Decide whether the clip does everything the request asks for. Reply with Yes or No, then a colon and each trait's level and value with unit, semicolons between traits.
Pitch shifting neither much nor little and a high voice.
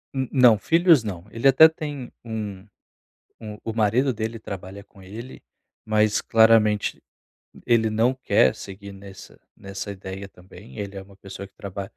No: average, 3.1 semitones; low, 105 Hz